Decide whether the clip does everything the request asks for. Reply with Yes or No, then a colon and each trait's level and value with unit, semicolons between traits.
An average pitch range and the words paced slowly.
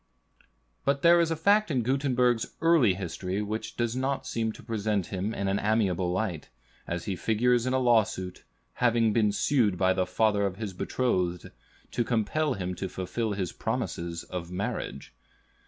No: average, 4.9 semitones; average, 170 wpm